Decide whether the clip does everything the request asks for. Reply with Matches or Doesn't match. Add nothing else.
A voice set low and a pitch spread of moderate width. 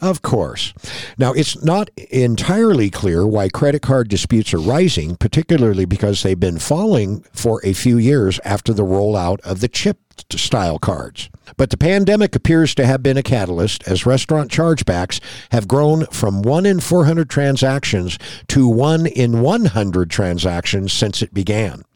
Doesn't match